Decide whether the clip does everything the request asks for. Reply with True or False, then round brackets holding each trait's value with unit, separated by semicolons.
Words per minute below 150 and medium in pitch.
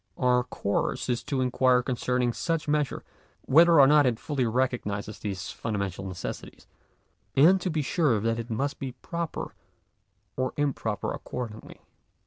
False (140 wpm; 125 Hz)